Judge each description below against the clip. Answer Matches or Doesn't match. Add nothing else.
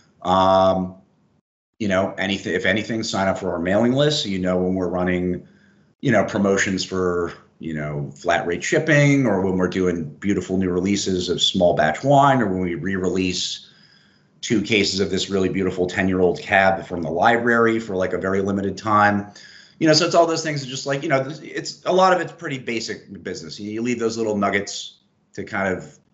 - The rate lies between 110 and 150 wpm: Doesn't match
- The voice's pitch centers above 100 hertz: Doesn't match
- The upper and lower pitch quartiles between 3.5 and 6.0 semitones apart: Matches